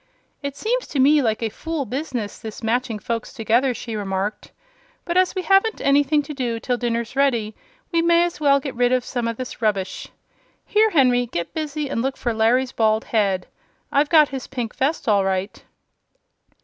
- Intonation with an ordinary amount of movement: Yes, average, 4.6 semitones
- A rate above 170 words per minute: Yes, average, 190 wpm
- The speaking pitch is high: Yes, very high, 250 Hz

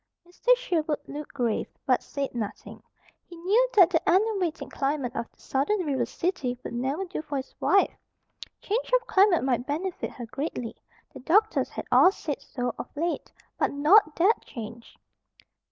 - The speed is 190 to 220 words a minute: No, average, 165 wpm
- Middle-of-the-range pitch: No, very high, 305 Hz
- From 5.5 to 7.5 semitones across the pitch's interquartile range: Yes, wide, 6.3 semitones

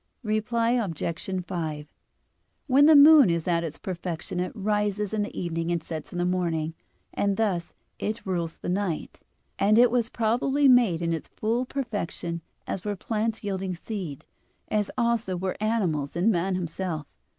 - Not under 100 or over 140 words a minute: No, average, 160 wpm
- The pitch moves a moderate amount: Yes, average, 4.7 semitones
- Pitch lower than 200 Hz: Yes, high, 190 Hz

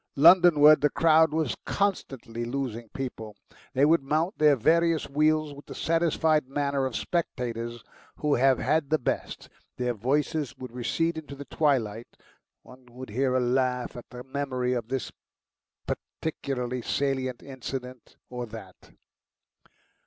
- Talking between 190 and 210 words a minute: No, average, 140 wpm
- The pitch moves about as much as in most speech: Yes, average, 3.7 semitones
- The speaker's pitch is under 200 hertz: Yes, low, 135 Hz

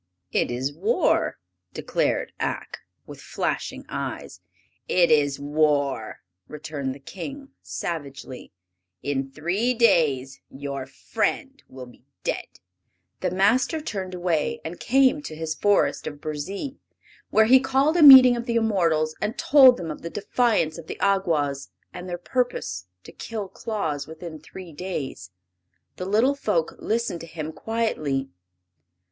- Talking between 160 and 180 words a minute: No, average, 140 wpm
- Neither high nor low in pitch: Yes, medium, 175 Hz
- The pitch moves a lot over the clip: Yes, wide, 7.8 semitones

